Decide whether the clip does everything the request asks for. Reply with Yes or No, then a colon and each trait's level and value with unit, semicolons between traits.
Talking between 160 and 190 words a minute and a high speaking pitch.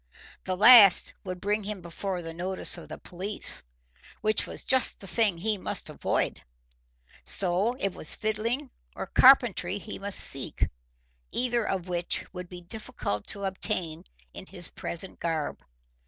No: average, 150 wpm; high, 195 Hz